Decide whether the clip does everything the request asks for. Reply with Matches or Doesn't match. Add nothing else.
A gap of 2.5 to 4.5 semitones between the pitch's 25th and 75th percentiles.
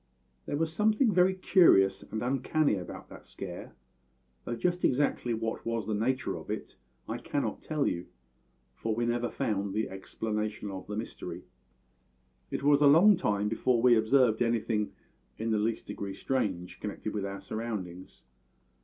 Doesn't match